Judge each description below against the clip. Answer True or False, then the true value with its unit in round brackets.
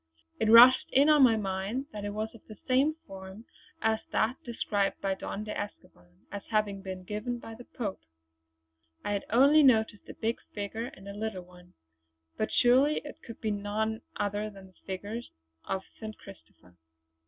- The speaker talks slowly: False (175 wpm)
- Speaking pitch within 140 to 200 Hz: False (215 Hz)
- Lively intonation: False (3.0 semitones)